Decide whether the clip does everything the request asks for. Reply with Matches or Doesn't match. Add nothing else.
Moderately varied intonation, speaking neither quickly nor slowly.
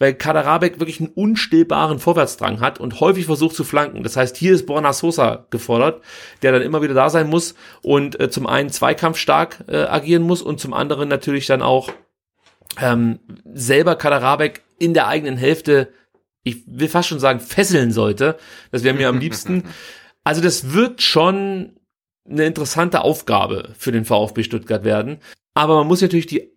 Matches